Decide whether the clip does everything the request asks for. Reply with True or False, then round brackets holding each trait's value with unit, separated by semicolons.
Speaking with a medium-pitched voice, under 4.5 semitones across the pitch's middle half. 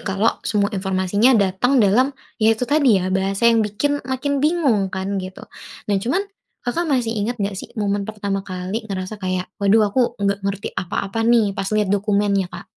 False (205 Hz; 3.3 semitones)